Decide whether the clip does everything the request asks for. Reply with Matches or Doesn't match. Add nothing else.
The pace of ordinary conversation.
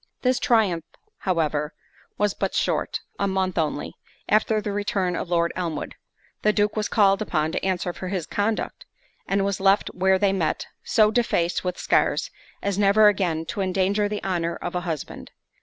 Matches